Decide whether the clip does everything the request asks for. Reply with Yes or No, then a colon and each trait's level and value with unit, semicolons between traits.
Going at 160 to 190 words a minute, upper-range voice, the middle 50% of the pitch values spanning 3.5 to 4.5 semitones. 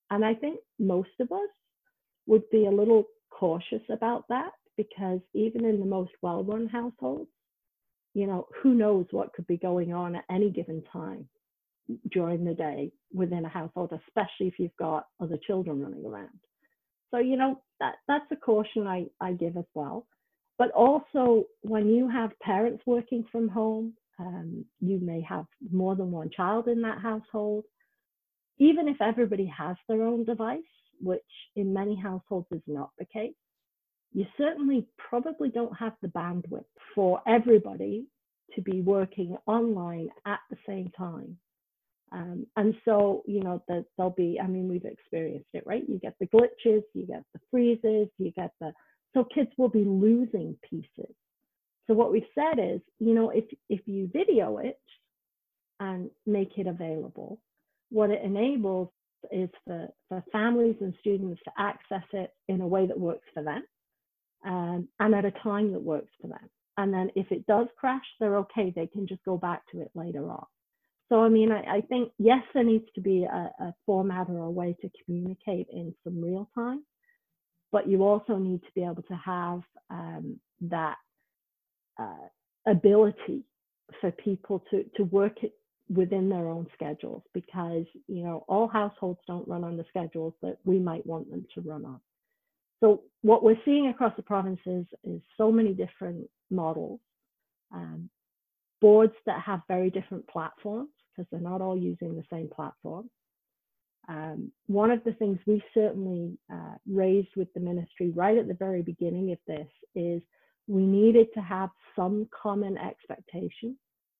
Yes: average, 170 wpm; high, 200 Hz; average, 4.1 semitones